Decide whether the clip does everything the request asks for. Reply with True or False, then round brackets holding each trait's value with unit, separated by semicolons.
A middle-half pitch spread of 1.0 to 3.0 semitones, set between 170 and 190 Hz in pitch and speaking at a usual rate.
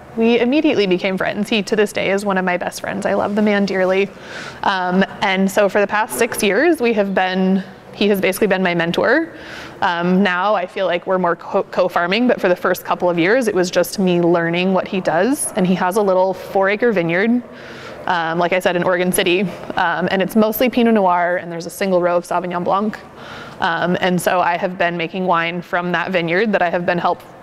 False (2.5 semitones; 185 Hz; 230 wpm)